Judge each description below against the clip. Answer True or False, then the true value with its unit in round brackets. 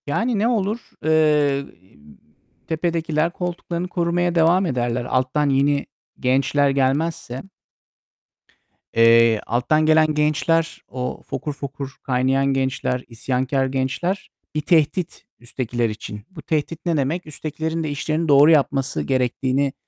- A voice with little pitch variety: False (3.7 semitones)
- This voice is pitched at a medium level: True (145 Hz)